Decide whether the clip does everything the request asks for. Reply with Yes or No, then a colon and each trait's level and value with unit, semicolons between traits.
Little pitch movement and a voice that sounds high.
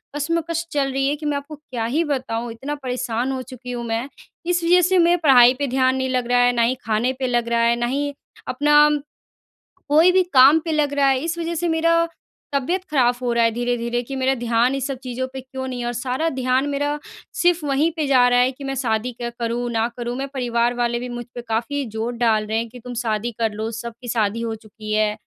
No: average, 3.2 semitones; very high, 255 Hz